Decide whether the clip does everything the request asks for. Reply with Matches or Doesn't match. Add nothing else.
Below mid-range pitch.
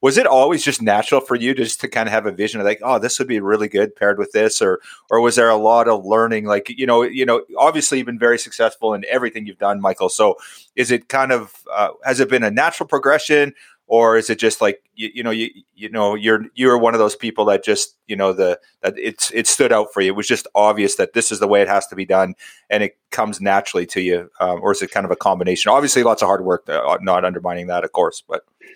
Matches